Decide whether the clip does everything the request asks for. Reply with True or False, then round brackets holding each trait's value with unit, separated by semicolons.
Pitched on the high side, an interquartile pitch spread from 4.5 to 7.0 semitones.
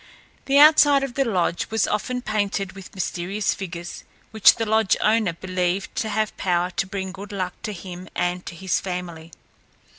False (195 Hz; 3.3 semitones)